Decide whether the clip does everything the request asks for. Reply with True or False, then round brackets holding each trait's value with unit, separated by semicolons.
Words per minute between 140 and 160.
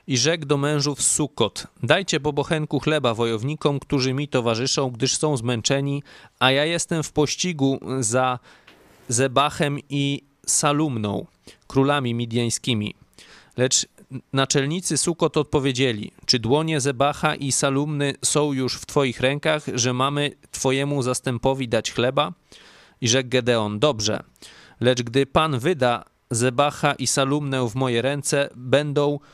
False (125 wpm)